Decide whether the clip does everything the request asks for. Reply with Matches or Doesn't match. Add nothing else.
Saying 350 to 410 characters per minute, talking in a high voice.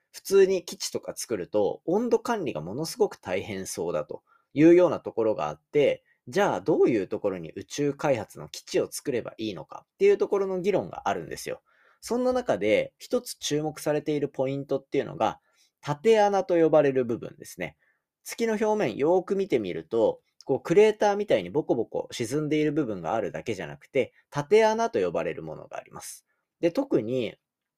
Matches